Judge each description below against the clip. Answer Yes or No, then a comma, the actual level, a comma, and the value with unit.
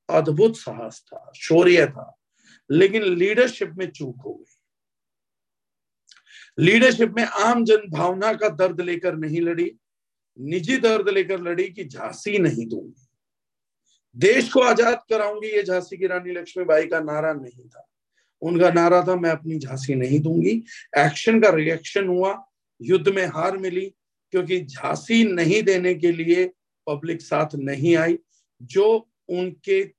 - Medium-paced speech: Yes, average, 140 wpm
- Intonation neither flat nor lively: Yes, average, 4.6 semitones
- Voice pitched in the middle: Yes, medium, 180 Hz